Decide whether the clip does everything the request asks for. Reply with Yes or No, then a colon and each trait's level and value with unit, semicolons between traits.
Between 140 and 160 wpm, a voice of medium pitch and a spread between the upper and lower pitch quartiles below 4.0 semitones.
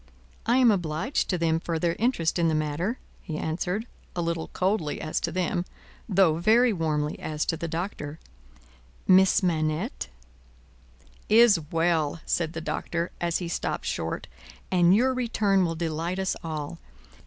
Yes: average, 155 wpm; medium, 170 Hz; average, 3.2 semitones